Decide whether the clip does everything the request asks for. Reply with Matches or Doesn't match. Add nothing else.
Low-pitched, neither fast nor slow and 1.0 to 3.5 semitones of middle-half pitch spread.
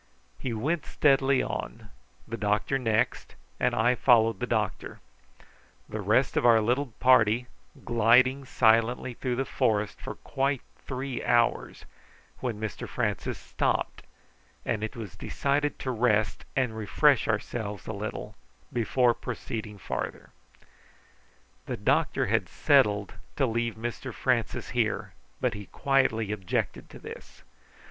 Doesn't match